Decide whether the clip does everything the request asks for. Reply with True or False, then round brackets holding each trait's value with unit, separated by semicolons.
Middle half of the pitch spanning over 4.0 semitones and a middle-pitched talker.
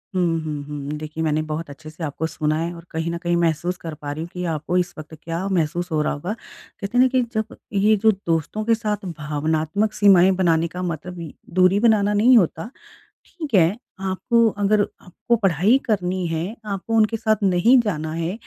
True (4.5 semitones; 180 Hz)